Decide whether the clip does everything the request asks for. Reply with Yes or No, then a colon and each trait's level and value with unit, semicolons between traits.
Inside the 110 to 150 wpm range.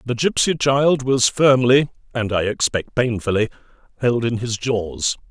Yes: average, 145 wpm